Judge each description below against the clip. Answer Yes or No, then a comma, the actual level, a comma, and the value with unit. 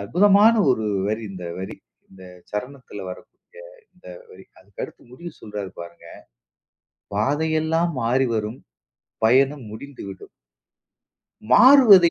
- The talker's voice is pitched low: Yes, low, 130 Hz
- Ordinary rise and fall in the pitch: No, wide, 8.3 semitones